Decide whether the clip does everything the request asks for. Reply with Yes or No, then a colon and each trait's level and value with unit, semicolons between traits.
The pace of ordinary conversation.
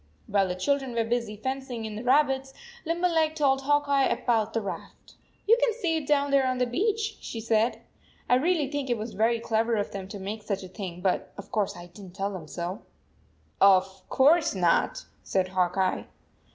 No: fast, 210 wpm